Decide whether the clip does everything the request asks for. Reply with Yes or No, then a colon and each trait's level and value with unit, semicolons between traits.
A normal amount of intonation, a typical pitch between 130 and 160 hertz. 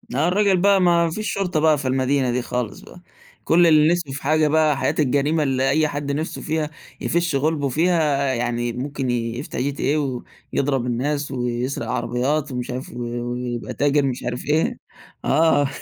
Yes: average, 3.6 semitones; medium, 140 Hz